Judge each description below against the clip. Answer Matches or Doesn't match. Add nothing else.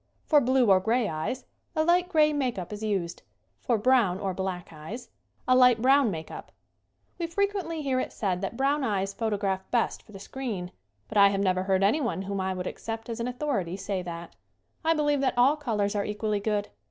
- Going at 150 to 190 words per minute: Doesn't match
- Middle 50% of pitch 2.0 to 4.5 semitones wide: Doesn't match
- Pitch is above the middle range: Matches